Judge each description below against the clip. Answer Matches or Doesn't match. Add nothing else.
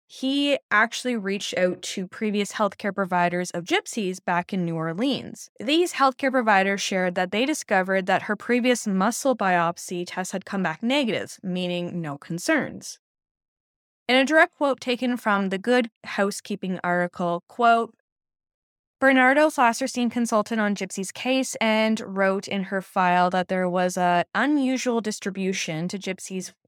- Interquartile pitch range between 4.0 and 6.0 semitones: Matches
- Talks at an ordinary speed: Matches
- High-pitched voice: Matches